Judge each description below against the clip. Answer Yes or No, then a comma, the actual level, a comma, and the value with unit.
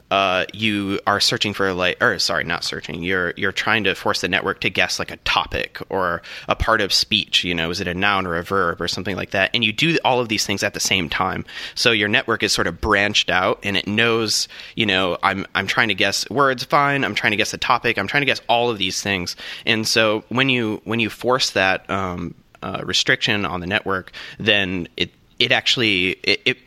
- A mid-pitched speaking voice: No, low, 100 Hz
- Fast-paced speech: Yes, fast, 235 wpm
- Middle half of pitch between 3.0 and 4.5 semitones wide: Yes, average, 3.4 semitones